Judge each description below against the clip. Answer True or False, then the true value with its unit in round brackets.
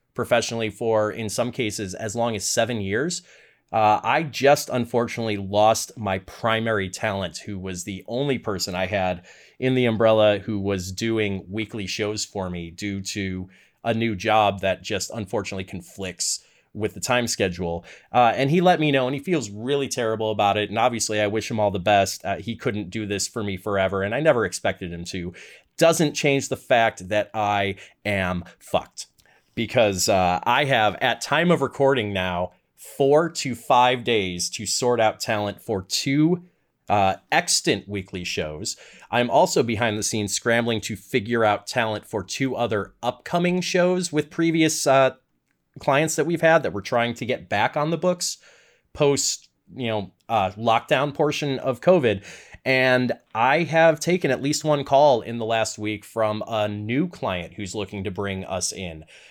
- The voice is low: True (110 Hz)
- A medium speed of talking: True (175 wpm)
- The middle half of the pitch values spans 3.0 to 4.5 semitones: False (4.9 semitones)